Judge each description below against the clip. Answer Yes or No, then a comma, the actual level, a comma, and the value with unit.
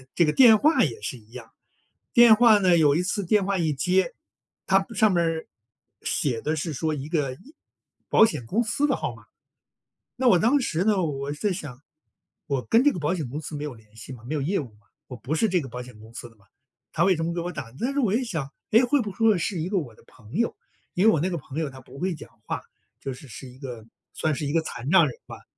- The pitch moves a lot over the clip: Yes, wide, 6.8 semitones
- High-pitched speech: No, medium, 160 Hz